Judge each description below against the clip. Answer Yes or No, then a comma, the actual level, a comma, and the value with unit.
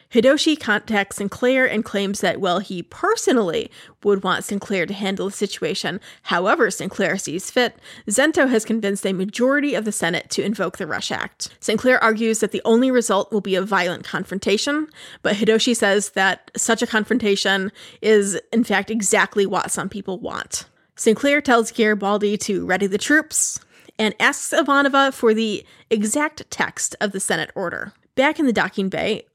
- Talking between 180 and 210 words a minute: No, average, 170 wpm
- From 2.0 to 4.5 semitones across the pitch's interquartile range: Yes, average, 3.6 semitones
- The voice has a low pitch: No, high, 215 Hz